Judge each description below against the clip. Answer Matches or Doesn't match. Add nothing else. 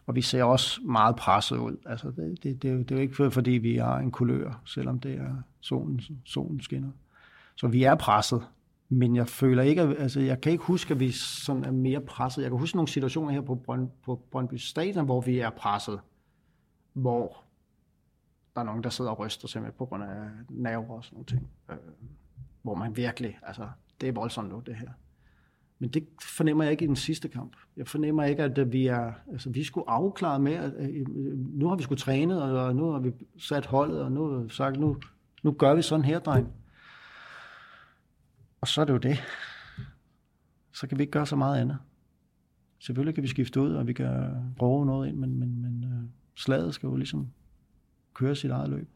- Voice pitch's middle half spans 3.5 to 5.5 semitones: Doesn't match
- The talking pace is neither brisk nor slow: Matches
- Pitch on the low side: Matches